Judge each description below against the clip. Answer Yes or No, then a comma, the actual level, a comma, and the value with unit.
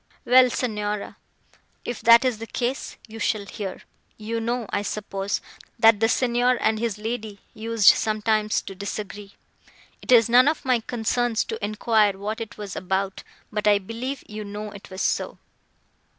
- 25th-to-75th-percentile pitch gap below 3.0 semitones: Yes, narrow, 2.4 semitones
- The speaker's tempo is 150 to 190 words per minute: Yes, average, 160 wpm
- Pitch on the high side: Yes, high, 220 Hz